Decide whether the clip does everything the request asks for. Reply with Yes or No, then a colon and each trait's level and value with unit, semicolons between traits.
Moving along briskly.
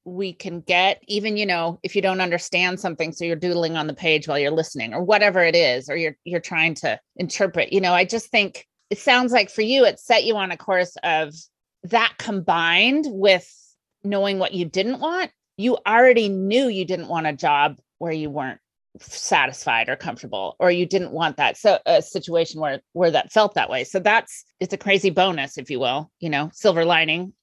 Yes: fast, 210 wpm